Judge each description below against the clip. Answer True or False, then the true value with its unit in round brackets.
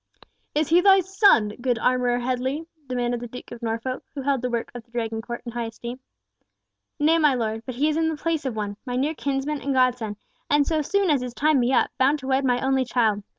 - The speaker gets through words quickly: True (240 wpm)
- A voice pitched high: True (255 Hz)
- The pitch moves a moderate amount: True (3.6 semitones)